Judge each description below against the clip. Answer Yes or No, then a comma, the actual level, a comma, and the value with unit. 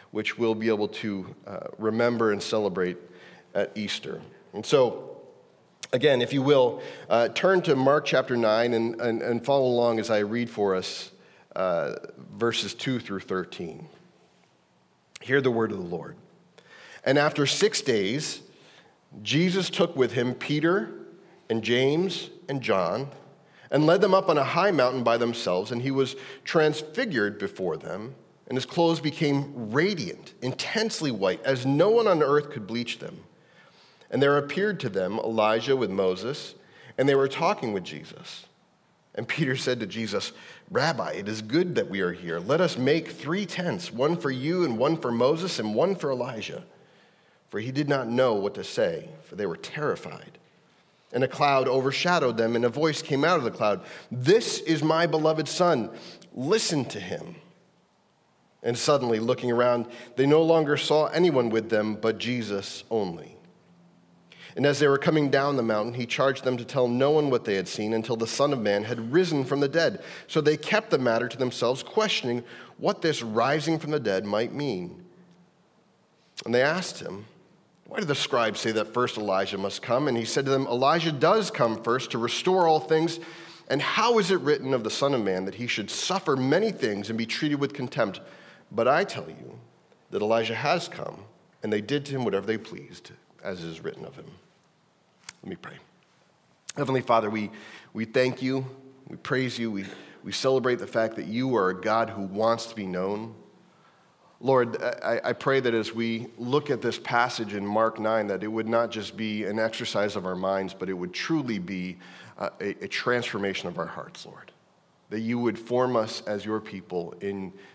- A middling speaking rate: Yes, average, 185 wpm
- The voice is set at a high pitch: No, low, 125 Hz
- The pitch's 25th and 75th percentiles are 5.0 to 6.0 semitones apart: Yes, average, 5.3 semitones